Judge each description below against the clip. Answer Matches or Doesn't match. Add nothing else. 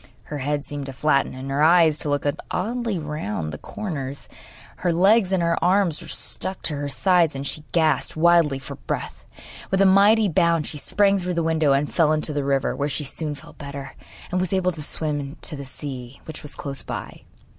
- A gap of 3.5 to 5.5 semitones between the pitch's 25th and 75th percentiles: Matches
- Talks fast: Matches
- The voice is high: Doesn't match